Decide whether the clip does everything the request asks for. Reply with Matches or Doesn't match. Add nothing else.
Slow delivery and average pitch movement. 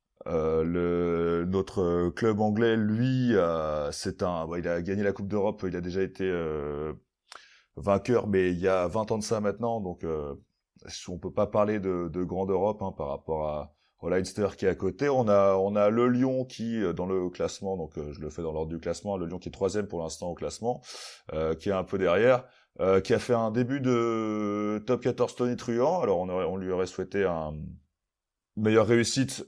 Doesn't match